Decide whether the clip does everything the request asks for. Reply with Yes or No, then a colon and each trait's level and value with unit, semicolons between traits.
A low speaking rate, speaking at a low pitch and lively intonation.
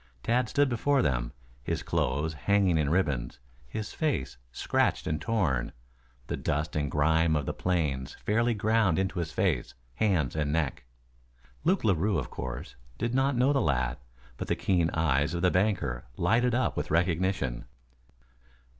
No: average, 155 wpm; very low, 85 Hz; wide, 7.0 semitones